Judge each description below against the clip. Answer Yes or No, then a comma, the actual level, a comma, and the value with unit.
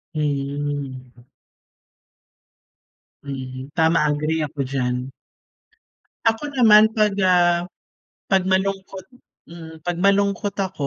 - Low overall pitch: No, medium, 165 Hz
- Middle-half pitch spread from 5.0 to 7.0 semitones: Yes, wide, 5.6 semitones